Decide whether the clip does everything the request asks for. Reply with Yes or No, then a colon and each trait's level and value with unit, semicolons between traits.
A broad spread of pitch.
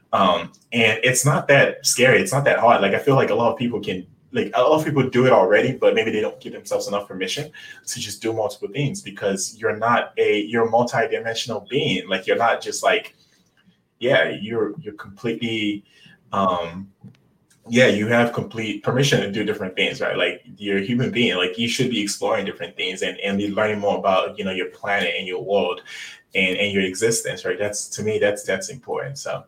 Yes: wide, 6.7 semitones